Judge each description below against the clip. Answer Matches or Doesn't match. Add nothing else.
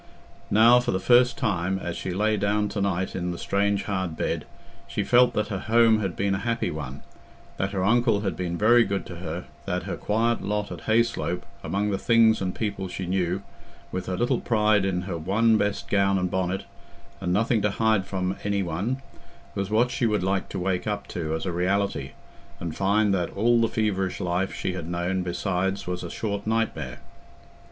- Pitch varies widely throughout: Doesn't match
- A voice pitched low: Matches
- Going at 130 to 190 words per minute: Doesn't match